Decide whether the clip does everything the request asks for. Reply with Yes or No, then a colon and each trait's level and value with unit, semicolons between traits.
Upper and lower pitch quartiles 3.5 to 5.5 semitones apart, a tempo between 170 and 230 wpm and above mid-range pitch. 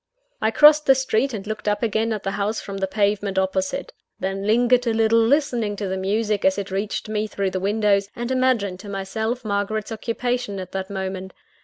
No: average, 2.7 semitones; average, 200 wpm; high, 210 Hz